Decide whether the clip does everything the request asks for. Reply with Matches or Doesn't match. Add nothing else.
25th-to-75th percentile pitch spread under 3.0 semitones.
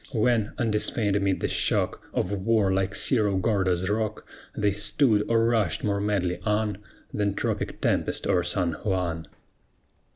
Matches